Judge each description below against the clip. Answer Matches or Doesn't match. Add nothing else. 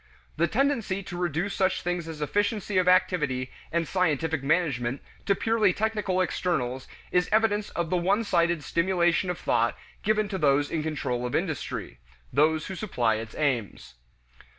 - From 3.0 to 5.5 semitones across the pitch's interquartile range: Matches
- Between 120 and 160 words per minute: Matches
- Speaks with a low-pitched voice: Doesn't match